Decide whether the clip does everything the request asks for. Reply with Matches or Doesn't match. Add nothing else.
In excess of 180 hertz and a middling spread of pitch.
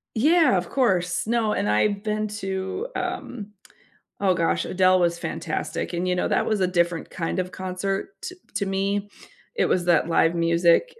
Matches